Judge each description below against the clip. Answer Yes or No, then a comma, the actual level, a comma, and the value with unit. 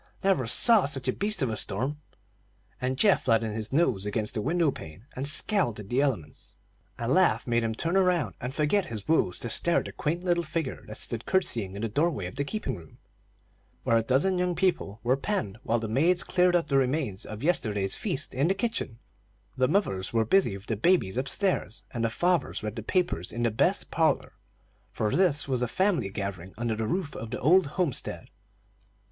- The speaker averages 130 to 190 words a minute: No, fast, 205 wpm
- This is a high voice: No, low, 130 Hz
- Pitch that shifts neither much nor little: No, wide, 7.8 semitones